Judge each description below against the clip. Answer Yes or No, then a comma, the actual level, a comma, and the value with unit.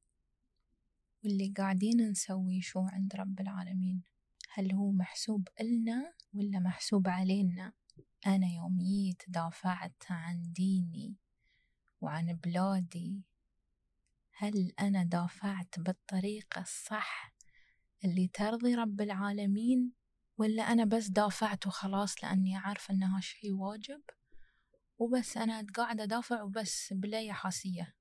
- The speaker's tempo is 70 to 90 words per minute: No, average, 105 wpm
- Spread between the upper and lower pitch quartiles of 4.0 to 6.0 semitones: No, narrow, 2.4 semitones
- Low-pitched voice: No, high, 195 Hz